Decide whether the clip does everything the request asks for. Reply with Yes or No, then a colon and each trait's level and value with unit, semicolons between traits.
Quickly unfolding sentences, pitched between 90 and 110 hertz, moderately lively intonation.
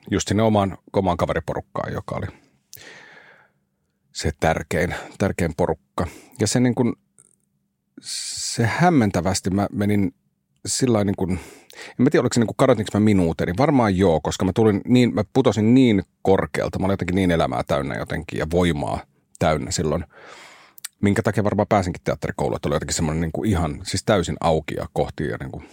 Yes: fast, 165 wpm; low, 100 Hz; average, 3.6 semitones